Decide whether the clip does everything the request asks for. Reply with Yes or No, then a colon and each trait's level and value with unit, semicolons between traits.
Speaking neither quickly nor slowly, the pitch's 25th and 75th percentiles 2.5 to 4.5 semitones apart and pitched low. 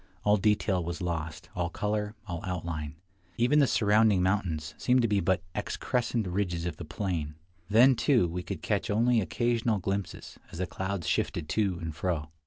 Yes: average, 180 wpm; average, 4.1 semitones; very low, 95 Hz